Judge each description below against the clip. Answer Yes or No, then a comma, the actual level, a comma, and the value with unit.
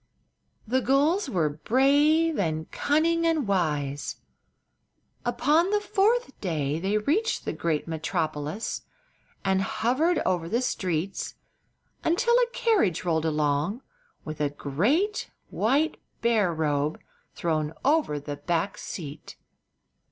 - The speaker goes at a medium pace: No, slow, 115 wpm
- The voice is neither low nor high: No, high, 200 Hz